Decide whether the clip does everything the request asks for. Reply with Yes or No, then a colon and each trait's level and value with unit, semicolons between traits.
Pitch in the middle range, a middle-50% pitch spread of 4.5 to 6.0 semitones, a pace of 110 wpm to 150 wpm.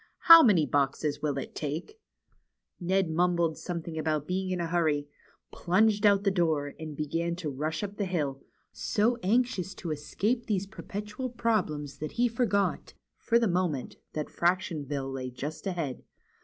No: medium, 175 Hz; average, 5.0 semitones; average, 160 wpm